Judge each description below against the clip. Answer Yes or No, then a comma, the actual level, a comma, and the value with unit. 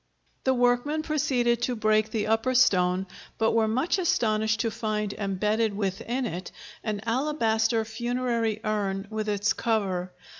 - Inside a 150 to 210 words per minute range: No, average, 140 wpm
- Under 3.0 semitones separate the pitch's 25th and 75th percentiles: Yes, narrow, 2.5 semitones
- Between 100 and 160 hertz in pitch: No, high, 220 Hz